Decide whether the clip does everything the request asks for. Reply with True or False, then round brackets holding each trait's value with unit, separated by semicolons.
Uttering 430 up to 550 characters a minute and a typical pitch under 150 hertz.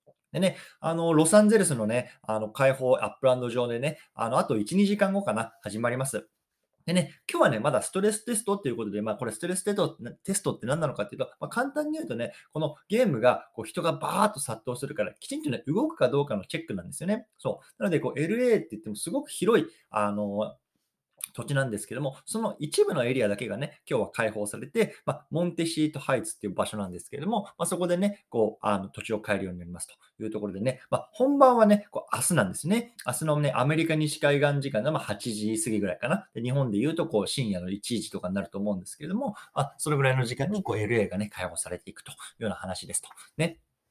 True (470 characters per minute; 140 Hz)